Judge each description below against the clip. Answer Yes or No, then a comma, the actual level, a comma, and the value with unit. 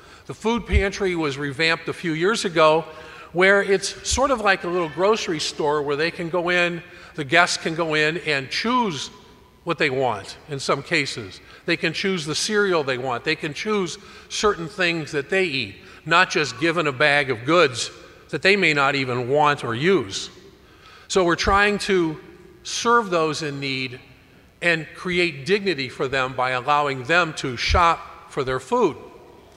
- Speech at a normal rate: Yes, average, 175 wpm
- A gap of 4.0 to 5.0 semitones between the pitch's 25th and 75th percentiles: Yes, average, 4.6 semitones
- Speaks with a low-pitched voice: No, medium, 165 Hz